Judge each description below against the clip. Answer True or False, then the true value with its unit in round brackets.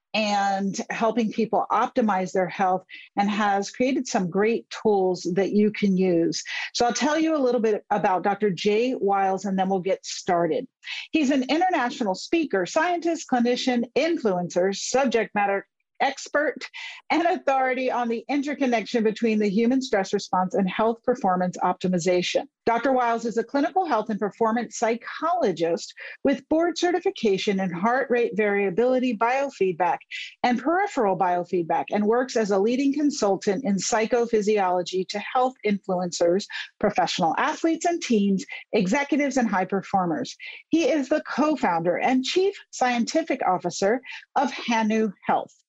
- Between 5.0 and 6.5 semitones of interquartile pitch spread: True (5.5 semitones)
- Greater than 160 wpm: False (140 wpm)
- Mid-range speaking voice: False (225 Hz)